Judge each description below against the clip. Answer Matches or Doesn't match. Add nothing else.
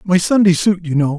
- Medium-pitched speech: Matches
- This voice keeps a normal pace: Doesn't match